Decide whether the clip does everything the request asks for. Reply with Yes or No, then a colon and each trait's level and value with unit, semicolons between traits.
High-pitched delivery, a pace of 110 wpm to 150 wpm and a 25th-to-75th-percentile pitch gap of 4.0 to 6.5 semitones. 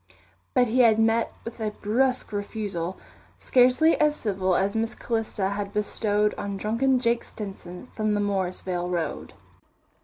No: high, 210 Hz; average, 145 wpm; average, 3.0 semitones